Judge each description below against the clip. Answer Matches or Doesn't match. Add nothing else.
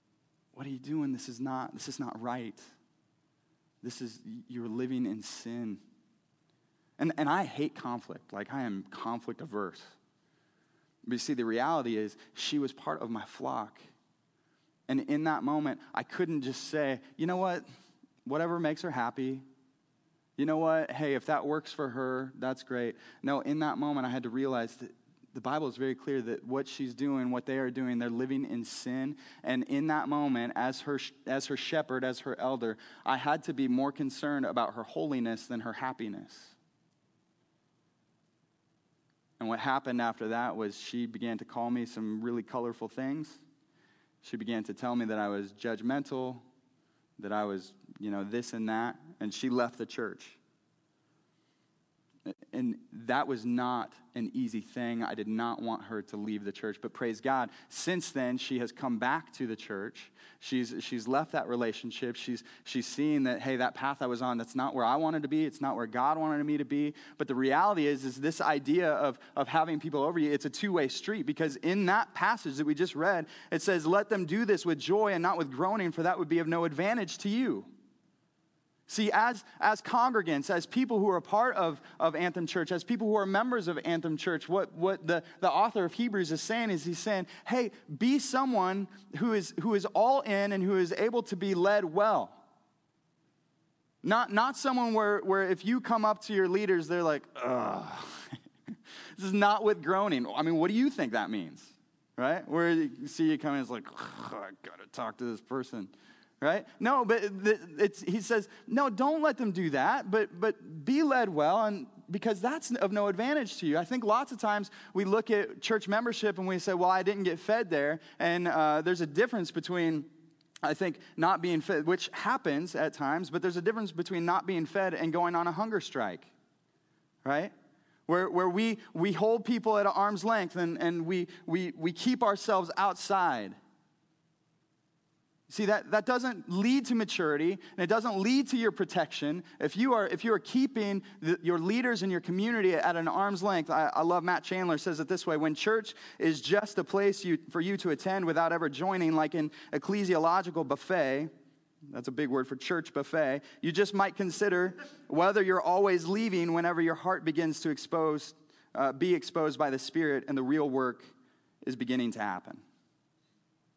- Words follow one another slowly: Doesn't match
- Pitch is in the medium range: Matches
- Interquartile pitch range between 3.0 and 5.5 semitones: Doesn't match